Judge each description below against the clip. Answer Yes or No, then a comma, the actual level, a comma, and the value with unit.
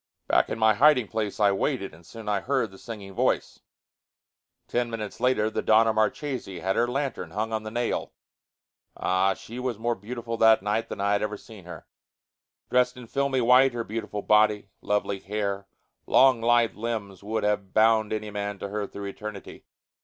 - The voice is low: Yes, low, 110 Hz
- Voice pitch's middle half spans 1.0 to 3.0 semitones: Yes, narrow, 2.6 semitones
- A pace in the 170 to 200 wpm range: Yes, average, 185 wpm